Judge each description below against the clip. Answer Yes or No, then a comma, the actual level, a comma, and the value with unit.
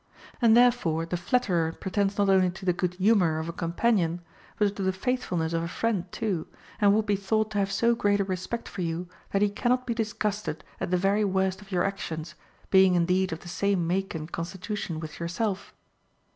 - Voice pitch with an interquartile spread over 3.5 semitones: No, average, 3.2 semitones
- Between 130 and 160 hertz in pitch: No, high, 190 Hz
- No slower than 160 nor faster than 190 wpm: No, fast, 205 wpm